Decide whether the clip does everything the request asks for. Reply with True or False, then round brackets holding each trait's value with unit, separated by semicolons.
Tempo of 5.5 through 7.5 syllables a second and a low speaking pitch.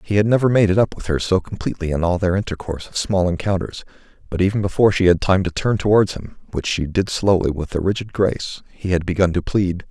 True (6.3 syllables/s; 95 Hz)